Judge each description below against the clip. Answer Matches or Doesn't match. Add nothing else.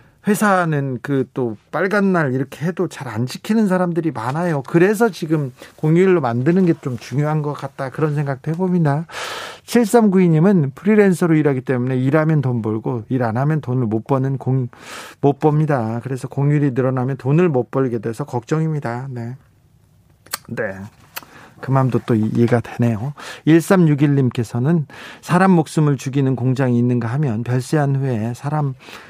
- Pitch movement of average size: Matches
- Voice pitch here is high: Doesn't match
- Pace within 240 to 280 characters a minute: Doesn't match